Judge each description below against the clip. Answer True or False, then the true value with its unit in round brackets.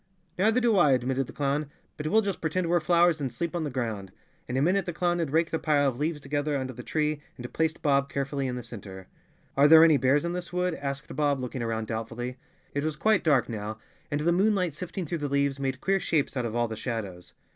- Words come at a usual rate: False (245 wpm)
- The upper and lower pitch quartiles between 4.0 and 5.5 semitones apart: True (4.8 semitones)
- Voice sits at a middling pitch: True (145 Hz)